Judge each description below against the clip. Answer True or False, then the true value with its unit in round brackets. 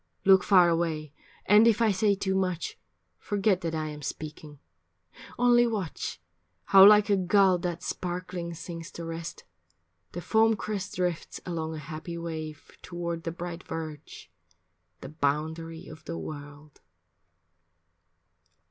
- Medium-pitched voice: True (170 Hz)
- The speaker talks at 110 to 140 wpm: True (135 wpm)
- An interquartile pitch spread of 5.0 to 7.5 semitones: False (3.3 semitones)